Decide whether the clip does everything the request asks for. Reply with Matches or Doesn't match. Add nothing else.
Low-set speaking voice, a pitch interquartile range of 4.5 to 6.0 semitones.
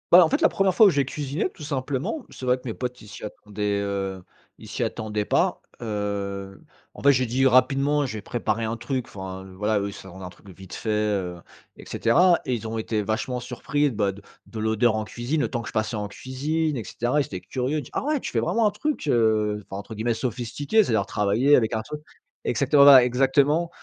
Matches